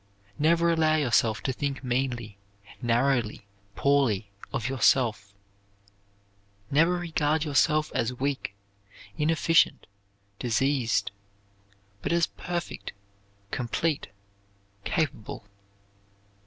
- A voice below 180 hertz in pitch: Yes, low, 135 Hz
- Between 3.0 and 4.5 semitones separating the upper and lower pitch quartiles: No, average, 4.9 semitones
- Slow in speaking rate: Yes, slow, 80 wpm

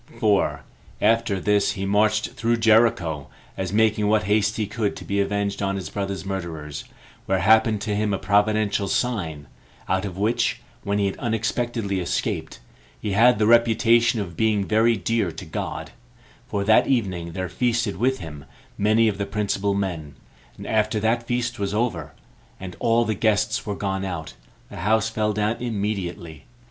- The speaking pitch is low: Yes, low, 105 Hz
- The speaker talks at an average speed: Yes, average, 170 wpm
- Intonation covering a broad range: No, narrow, 2.5 semitones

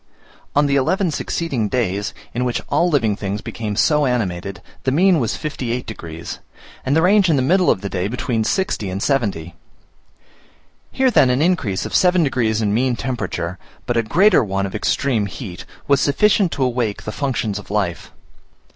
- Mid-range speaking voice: No, low, 125 Hz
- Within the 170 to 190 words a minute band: Yes, average, 180 wpm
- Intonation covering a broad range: Yes, wide, 6.1 semitones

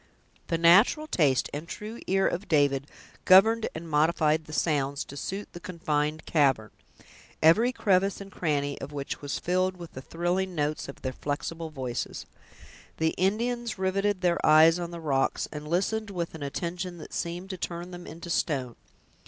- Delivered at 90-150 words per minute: No, average, 170 wpm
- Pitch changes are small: No, average, 4.0 semitones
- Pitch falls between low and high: Yes, medium, 170 Hz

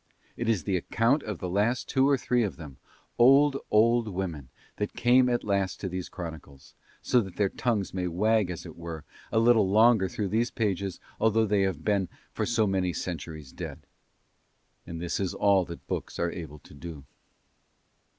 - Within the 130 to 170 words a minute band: No, average, 185 wpm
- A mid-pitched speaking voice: No, low, 100 Hz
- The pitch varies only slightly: No, average, 4.7 semitones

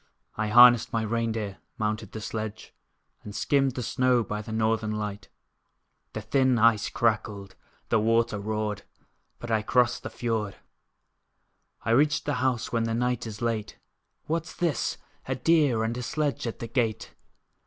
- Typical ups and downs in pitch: No, narrow, 2.3 semitones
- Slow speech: No, average, 160 wpm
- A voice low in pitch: Yes, low, 115 Hz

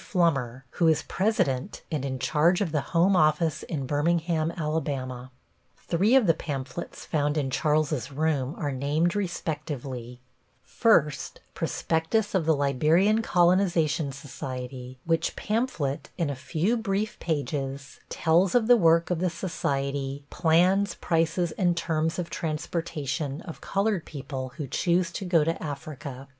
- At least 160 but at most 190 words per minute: No, average, 140 wpm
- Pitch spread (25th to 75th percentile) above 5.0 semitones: No, average, 3.9 semitones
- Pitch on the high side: No, medium, 160 Hz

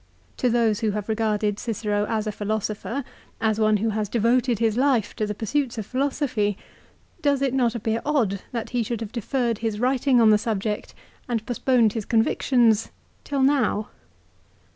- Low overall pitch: No, high, 225 Hz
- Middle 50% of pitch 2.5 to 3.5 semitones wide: Yes, average, 2.8 semitones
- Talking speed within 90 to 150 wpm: No, average, 175 wpm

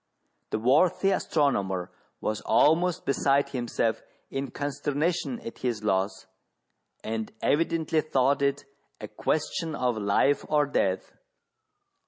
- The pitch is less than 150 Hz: Yes, medium, 140 Hz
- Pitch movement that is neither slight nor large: No, wide, 5.7 semitones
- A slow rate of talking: Yes, slow, 110 wpm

